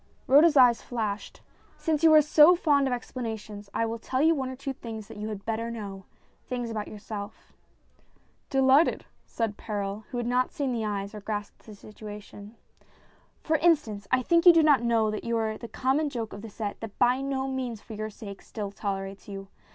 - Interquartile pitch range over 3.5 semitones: Yes, average, 4.1 semitones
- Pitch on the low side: No, high, 230 Hz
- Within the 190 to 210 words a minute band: Yes, fast, 205 wpm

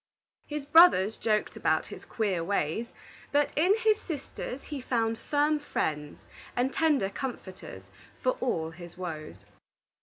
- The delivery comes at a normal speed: No, slow, 130 wpm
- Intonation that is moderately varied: No, wide, 8.0 semitones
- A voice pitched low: No, high, 235 Hz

